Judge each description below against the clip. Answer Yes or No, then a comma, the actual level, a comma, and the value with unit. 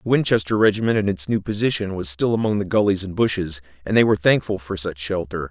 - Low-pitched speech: Yes, very low, 95 Hz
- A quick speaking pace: Yes, fast, 230 wpm